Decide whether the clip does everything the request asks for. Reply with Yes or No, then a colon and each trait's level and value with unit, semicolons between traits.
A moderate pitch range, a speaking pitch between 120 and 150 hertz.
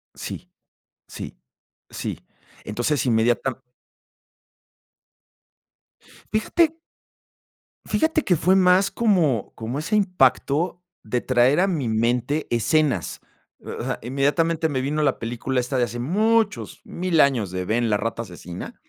No: wide, 7.0 semitones; medium, 140 Hz